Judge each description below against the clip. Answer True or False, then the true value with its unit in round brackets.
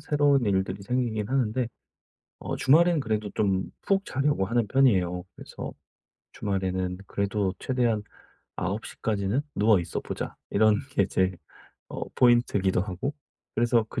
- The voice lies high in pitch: False (110 Hz)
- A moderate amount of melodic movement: True (4.8 semitones)